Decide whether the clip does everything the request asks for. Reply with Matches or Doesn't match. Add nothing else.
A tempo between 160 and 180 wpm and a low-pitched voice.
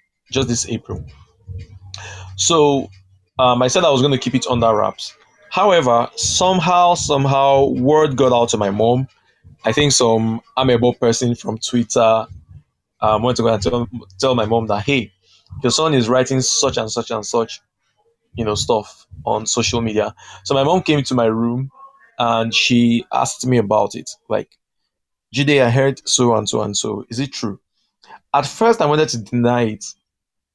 Matches